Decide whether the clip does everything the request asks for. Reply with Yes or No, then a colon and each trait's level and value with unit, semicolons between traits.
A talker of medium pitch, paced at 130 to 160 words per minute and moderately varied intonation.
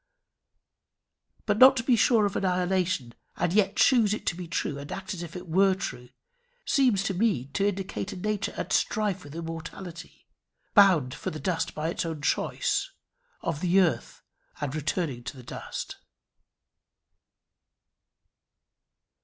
Yes: medium, 180 Hz; average, 150 wpm; average, 4.0 semitones